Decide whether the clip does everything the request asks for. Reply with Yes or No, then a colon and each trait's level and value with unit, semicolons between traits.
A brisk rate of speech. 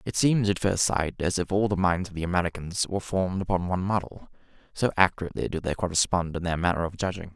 Yes: fast, 230 wpm